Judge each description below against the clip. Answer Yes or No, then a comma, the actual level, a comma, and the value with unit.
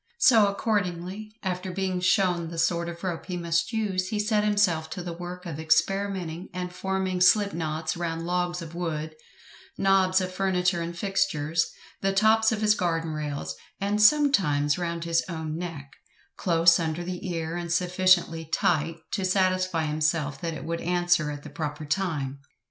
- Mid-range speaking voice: Yes, medium, 175 Hz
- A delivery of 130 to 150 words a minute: No, average, 165 wpm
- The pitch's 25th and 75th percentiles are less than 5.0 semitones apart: Yes, average, 2.7 semitones